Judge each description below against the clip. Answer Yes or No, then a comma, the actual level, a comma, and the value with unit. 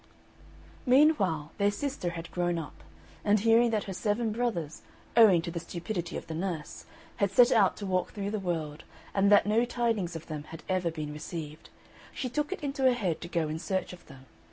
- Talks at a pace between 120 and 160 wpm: No, average, 200 wpm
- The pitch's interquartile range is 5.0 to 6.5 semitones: Yes, average, 5.3 semitones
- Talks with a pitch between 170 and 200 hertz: Yes, high, 190 Hz